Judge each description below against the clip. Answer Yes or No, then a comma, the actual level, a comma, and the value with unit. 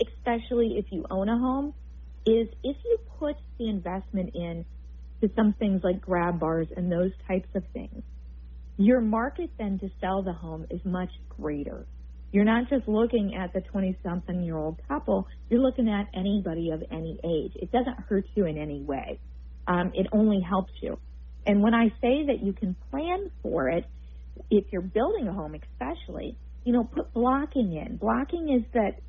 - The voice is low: No, high, 195 Hz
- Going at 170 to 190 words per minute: Yes, average, 180 wpm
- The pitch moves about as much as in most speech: No, wide, 6.0 semitones